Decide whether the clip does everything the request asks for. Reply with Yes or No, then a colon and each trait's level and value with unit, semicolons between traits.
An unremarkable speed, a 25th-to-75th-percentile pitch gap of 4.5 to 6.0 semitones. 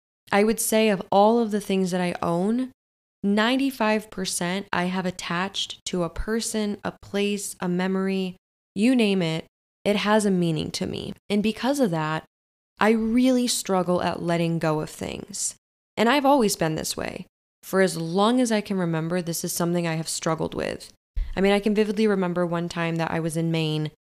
No: average, 190 wpm; average, 3.8 semitones